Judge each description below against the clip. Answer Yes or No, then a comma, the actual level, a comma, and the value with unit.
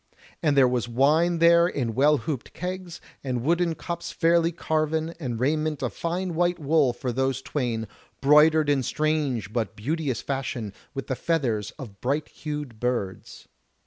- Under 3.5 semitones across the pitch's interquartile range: No, average, 4.6 semitones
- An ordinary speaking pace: Yes, average, 155 wpm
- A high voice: No, medium, 145 Hz